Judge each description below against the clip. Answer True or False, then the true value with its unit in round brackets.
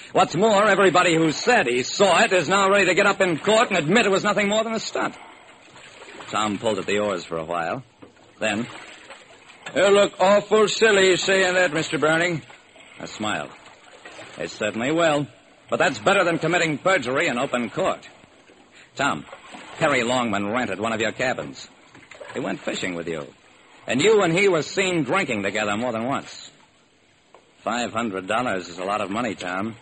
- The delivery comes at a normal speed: True (175 wpm)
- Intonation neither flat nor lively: False (8.5 semitones)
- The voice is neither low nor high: True (170 Hz)